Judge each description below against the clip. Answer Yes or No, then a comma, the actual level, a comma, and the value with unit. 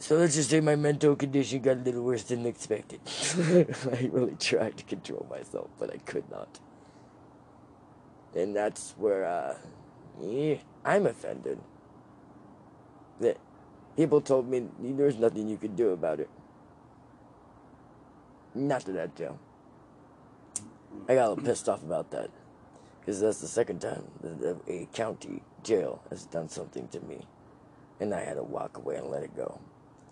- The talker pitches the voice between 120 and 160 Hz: Yes, low, 135 Hz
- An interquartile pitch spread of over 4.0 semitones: No, average, 3.3 semitones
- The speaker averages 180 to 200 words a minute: No, average, 150 wpm